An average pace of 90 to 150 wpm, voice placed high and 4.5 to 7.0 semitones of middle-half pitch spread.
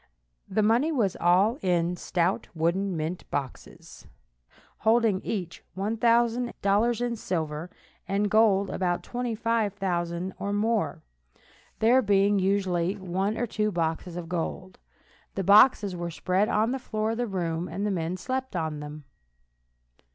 No: slow, 135 wpm; high, 195 Hz; average, 4.1 semitones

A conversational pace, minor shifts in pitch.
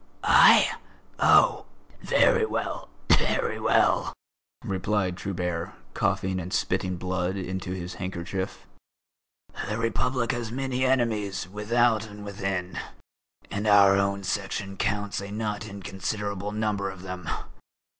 No: slow, 115 wpm; narrow, 2.3 semitones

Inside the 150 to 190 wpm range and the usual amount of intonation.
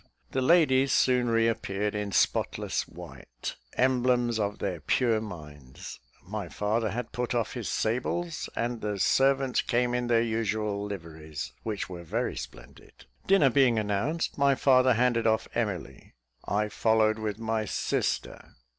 No: average, 140 wpm; average, 3.4 semitones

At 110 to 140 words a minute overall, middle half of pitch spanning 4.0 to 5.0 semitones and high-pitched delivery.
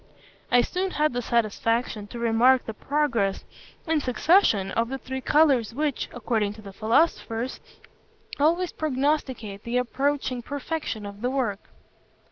Yes: slow, 135 wpm; average, 4.4 semitones; very high, 250 Hz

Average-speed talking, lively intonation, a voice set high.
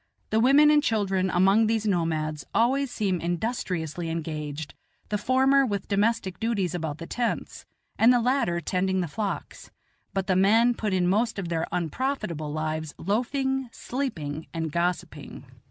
Yes: average, 150 wpm; wide, 5.8 semitones; high, 195 Hz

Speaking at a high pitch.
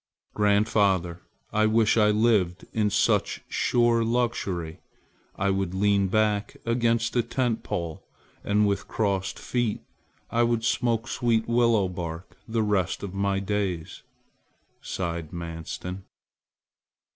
No: low, 105 Hz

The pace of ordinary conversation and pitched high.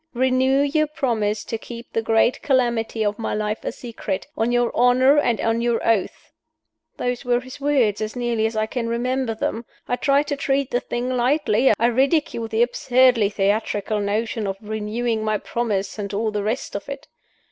Yes: average, 185 wpm; high, 235 Hz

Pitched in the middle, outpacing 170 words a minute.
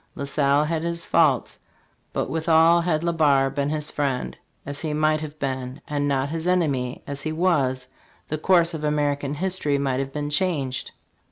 Yes: medium, 150 Hz; average, 180 wpm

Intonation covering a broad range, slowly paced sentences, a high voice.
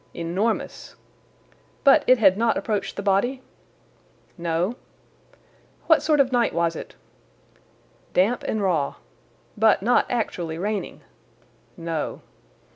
Yes: wide, 5.9 semitones; slow, 110 wpm; high, 205 Hz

